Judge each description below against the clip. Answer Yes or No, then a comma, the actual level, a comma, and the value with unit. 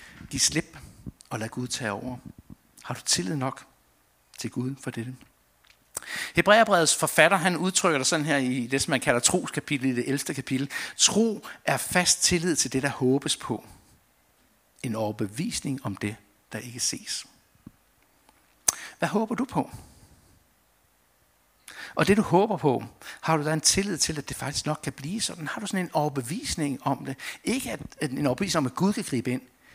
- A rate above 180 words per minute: No, average, 175 wpm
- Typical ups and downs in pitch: No, wide, 6.3 semitones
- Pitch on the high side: No, low, 135 Hz